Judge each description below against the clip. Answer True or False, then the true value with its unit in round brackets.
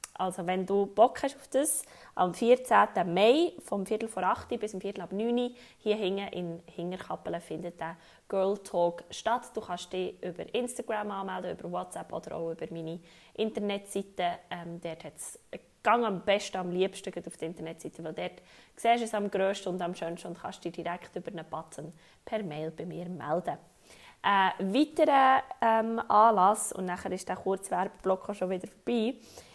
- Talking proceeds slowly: False (180 wpm)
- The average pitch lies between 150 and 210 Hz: True (190 Hz)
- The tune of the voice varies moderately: True (4.0 semitones)